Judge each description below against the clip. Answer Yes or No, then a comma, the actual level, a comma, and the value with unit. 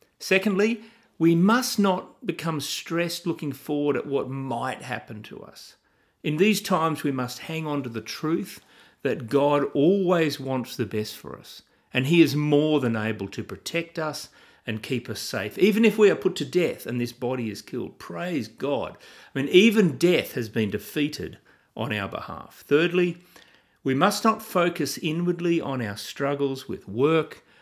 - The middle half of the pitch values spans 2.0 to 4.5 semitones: No, wide, 5.4 semitones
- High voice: No, medium, 155 Hz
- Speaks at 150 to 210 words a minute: Yes, average, 175 wpm